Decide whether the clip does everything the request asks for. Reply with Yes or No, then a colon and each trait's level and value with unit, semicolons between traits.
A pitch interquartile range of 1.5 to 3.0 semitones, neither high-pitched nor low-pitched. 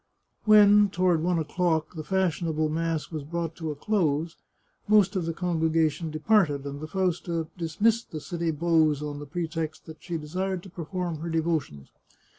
Yes: narrow, 2.6 semitones; medium, 165 Hz